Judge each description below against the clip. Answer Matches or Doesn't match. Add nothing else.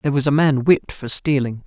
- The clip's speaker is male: Matches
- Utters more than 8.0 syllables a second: Doesn't match